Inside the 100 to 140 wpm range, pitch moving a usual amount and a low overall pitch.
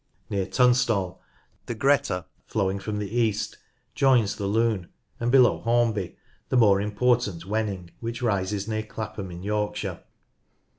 Yes: slow, 135 wpm; average, 3.2 semitones; low, 105 Hz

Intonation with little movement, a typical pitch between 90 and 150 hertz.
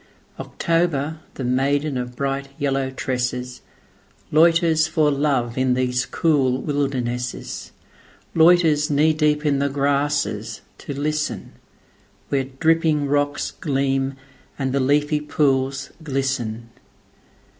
Yes: narrow, 2.3 semitones; medium, 140 Hz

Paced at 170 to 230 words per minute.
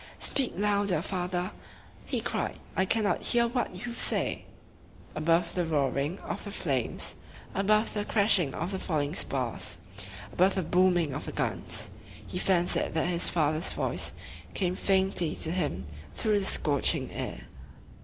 No: average, 145 wpm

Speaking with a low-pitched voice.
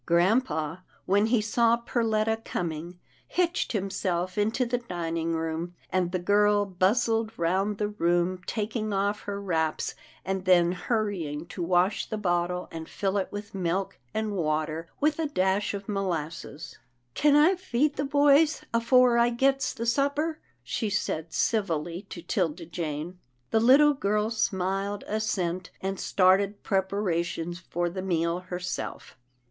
No: high, 195 Hz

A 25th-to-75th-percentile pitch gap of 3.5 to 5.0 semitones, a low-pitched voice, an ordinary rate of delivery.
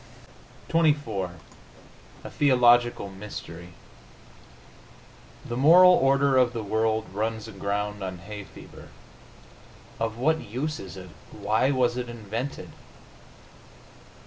No: average, 4.3 semitones; low, 115 Hz; slow, 100 wpm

